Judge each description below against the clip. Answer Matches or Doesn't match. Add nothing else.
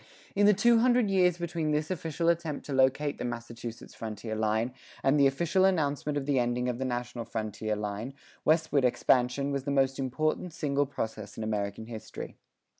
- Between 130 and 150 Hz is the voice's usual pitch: Matches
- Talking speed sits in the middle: Matches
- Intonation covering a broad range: Doesn't match